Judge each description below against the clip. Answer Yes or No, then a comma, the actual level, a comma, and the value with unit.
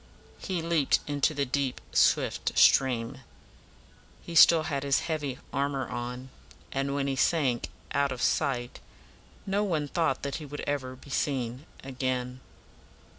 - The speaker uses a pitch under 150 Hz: Yes, medium, 140 Hz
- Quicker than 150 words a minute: No, average, 145 wpm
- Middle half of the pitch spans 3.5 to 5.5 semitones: No, narrow, 2.5 semitones